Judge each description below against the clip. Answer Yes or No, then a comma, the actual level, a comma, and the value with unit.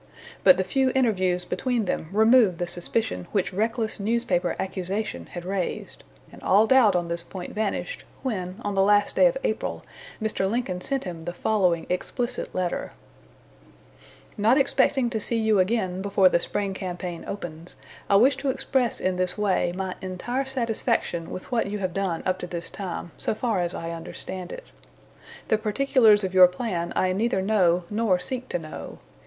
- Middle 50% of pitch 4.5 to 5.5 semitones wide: No, average, 4.0 semitones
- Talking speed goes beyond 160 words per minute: Yes, average, 175 wpm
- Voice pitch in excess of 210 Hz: No, high, 195 Hz